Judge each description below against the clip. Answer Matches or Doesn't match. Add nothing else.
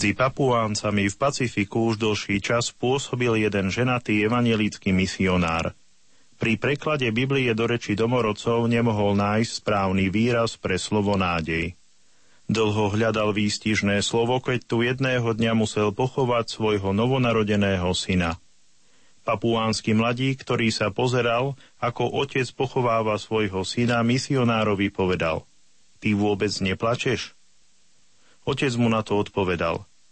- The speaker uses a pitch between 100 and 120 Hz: Matches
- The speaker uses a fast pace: Doesn't match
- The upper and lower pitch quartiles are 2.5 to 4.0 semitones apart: Matches